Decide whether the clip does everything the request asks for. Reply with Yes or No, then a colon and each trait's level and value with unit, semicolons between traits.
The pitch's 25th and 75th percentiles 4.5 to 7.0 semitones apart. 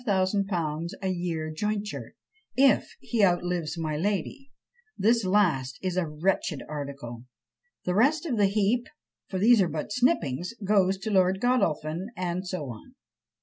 Yes: average, 4.8 semitones